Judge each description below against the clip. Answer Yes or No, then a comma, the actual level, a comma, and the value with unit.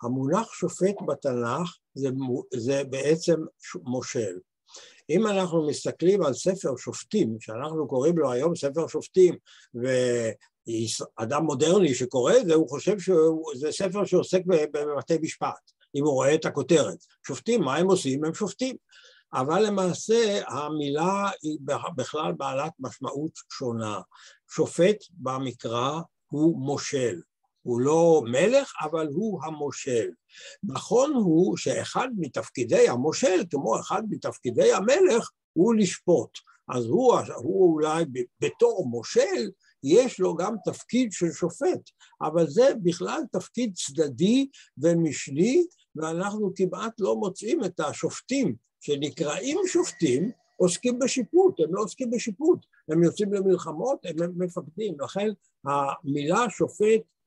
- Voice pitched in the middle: Yes, medium, 170 Hz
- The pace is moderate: Yes, average, 115 wpm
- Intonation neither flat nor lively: No, wide, 6.4 semitones